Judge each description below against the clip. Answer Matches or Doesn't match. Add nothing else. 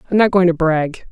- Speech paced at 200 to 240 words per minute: Doesn't match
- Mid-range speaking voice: Matches